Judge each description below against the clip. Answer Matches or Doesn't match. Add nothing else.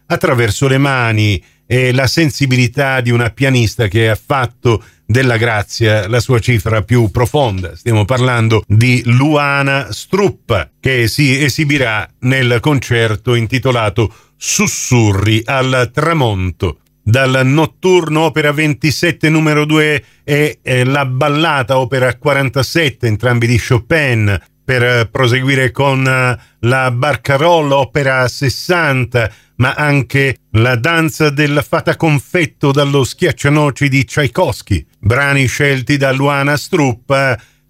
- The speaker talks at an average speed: Doesn't match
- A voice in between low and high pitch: Doesn't match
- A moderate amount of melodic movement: Matches